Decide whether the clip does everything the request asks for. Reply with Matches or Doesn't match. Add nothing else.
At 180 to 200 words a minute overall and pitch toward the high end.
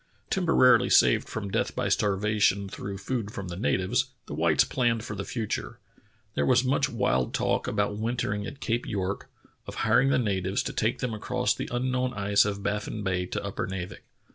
Doesn't match